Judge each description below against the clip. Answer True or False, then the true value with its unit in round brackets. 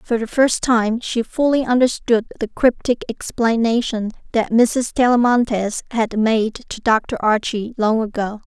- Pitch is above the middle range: True (230 Hz)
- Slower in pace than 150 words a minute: True (140 wpm)